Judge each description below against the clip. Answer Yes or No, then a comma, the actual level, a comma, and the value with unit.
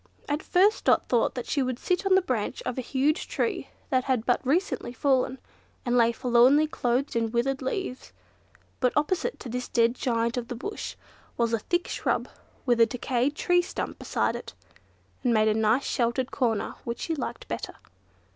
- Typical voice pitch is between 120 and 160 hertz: No, very high, 250 Hz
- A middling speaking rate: Yes, average, 185 wpm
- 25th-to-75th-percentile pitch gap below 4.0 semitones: Yes, average, 3.4 semitones